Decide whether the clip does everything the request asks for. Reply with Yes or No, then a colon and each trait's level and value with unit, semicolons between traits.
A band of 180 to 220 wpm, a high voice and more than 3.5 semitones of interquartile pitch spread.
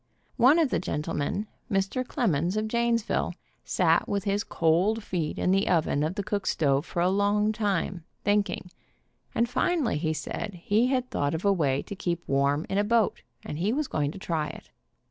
Yes: average, 195 wpm; high, 195 Hz; average, 5.0 semitones